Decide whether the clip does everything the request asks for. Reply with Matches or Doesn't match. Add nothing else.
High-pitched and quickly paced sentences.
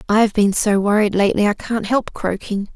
Doesn't match